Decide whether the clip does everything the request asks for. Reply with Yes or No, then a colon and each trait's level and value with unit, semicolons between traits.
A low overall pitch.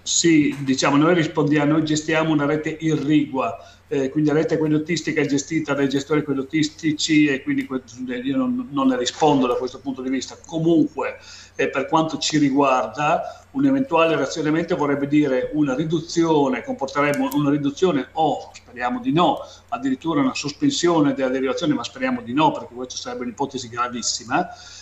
No: medium, 150 Hz